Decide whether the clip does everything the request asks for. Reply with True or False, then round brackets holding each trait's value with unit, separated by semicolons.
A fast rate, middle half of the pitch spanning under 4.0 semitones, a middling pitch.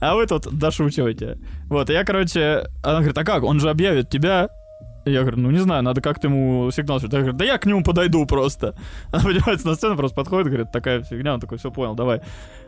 False (225 wpm; 4.3 semitones; 145 Hz)